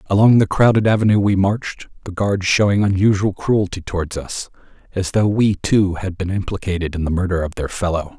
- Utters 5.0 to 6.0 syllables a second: Yes, 5.5 syllables/s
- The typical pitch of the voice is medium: No, very low, 95 Hz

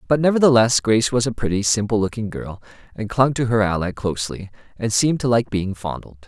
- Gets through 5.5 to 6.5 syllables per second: Yes, 6.0 syllables/s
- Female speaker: No, male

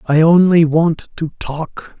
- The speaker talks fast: No, average, 150 wpm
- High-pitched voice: No, medium, 160 Hz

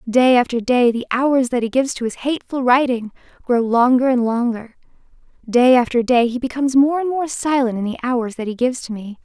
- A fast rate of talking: Yes, fast, 215 wpm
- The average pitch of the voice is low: No, very high, 250 Hz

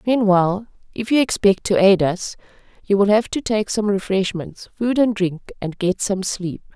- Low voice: No, high, 200 Hz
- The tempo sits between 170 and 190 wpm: Yes, average, 185 wpm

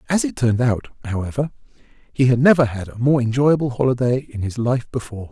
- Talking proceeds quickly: No, average, 190 wpm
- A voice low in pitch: Yes, low, 125 Hz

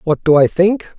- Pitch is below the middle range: No, medium, 180 Hz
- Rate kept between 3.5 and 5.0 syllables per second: Yes, 4.5 syllables/s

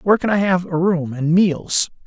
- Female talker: No, male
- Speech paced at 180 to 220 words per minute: No, fast, 235 wpm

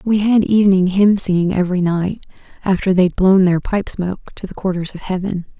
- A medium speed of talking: Yes, average, 195 wpm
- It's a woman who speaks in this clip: Yes, female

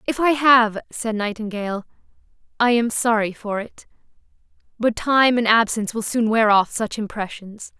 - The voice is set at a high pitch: Yes, high, 225 Hz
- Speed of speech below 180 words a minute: Yes, average, 155 wpm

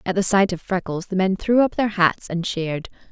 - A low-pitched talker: No, high, 190 Hz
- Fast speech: Yes, fast, 250 wpm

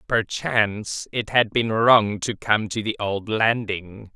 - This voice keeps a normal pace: Yes, average, 160 wpm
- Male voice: Yes, male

